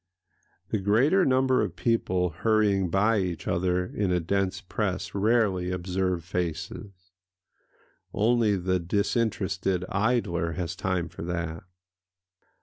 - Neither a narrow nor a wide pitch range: Yes, average, 3.1 semitones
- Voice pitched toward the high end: No, very low, 95 Hz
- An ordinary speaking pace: No, slow, 115 wpm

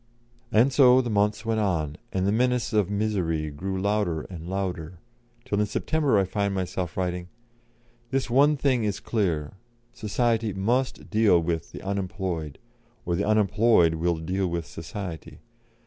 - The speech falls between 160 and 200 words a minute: No, average, 150 wpm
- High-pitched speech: No, low, 100 Hz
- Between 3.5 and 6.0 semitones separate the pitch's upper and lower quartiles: Yes, average, 4.1 semitones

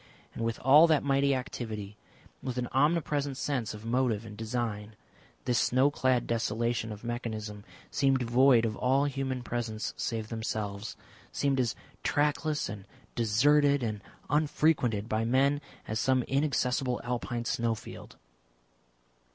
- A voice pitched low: Yes, low, 120 Hz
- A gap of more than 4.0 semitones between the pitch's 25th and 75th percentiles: No, average, 3.6 semitones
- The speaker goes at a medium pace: No, slow, 130 wpm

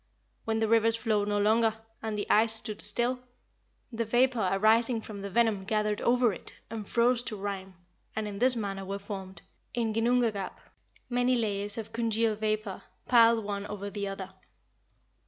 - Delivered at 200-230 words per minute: No, average, 165 wpm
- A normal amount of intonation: No, narrow, 2.2 semitones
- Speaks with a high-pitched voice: Yes, high, 220 Hz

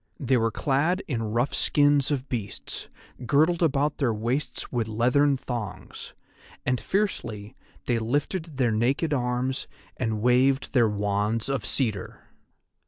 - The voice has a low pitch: Yes, low, 125 Hz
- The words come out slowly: Yes, slow, 130 wpm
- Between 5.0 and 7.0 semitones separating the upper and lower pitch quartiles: No, average, 4.0 semitones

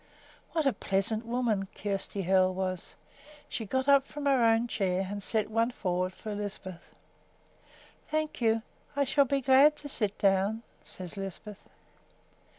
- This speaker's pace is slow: No, average, 150 wpm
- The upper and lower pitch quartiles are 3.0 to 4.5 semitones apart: No, average, 5.3 semitones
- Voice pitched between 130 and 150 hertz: No, high, 220 Hz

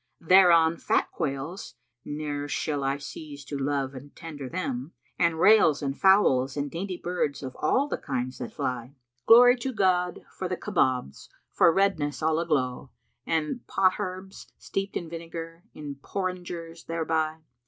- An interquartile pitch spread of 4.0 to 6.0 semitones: Yes, average, 4.3 semitones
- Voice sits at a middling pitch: Yes, medium, 160 Hz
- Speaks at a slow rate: No, average, 155 wpm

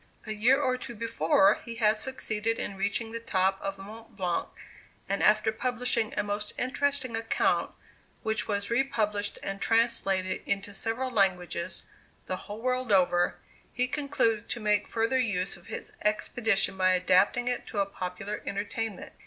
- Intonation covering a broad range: No, average, 3.0 semitones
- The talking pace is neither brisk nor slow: Yes, average, 160 wpm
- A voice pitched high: Yes, high, 210 Hz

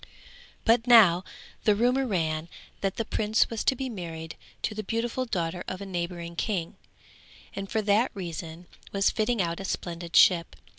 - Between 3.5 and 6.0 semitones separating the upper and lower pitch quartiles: Yes, average, 4.7 semitones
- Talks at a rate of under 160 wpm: No, average, 165 wpm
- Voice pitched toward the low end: No, high, 195 Hz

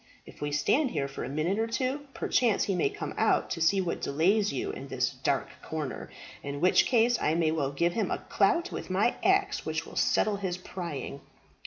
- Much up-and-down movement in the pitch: Yes, wide, 7.3 semitones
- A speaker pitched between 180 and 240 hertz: Yes, high, 190 Hz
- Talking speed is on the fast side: Yes, fast, 210 wpm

